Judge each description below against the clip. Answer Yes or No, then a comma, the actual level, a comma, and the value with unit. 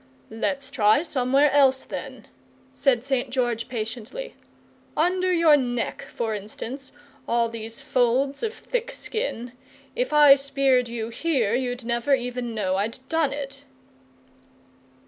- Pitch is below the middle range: No, very high, 260 Hz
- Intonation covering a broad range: No, average, 3.5 semitones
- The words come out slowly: Yes, slow, 125 wpm